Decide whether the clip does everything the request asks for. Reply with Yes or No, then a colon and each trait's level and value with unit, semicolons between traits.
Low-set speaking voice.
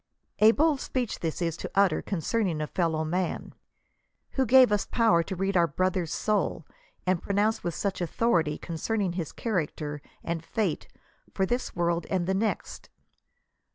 No: medium, 185 Hz